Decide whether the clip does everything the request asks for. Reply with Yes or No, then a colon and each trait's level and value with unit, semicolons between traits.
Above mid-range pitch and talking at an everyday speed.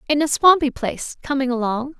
Yes: very high, 270 Hz; average, 180 wpm